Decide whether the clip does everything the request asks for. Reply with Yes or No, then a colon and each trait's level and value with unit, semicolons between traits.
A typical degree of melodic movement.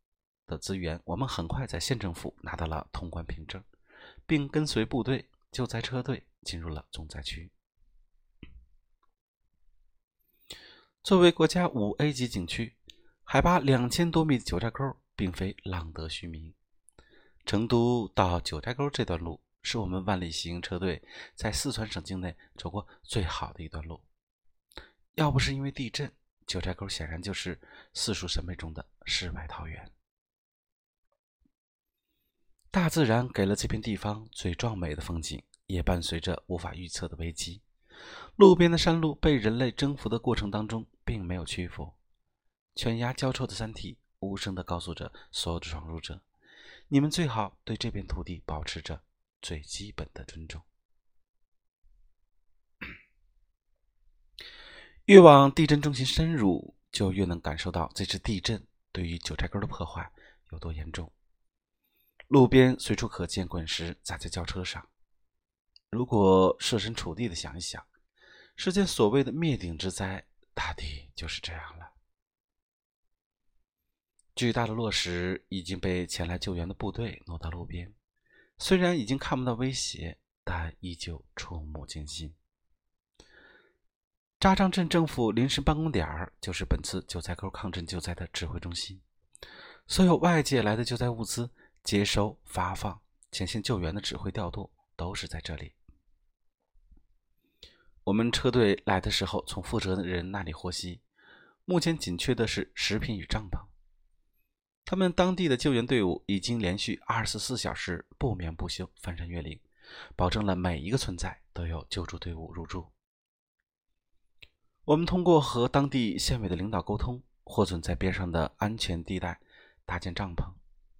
No: wide, 6.0 semitones